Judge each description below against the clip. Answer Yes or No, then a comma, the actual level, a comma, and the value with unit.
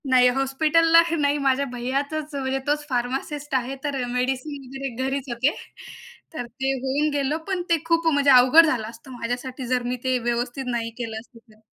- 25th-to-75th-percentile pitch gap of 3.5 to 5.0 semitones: No, average, 2.8 semitones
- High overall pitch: Yes, very high, 265 Hz